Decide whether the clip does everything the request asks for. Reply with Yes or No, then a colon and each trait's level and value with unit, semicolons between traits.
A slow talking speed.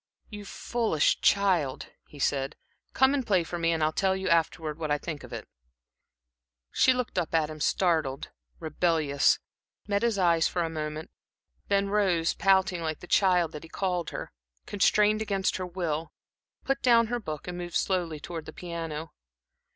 No: average, 175 wpm